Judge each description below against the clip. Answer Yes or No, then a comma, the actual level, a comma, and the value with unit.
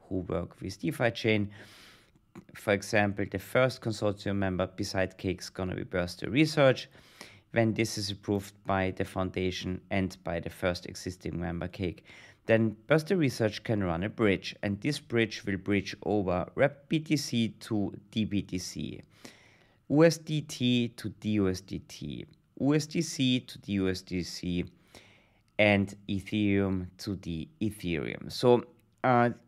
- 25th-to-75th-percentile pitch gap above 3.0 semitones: Yes, average, 3.9 semitones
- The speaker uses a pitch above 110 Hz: No, low, 100 Hz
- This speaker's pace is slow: Yes, slow, 130 wpm